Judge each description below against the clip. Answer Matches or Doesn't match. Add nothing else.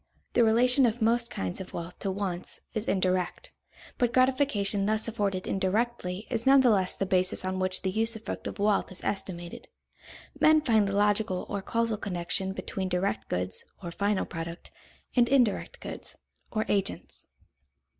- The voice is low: Doesn't match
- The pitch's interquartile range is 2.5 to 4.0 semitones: Matches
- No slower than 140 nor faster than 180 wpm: Matches